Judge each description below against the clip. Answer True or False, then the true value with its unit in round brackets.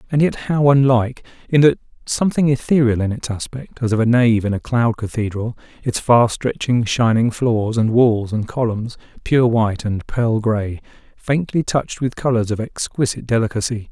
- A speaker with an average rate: True (170 wpm)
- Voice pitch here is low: True (120 Hz)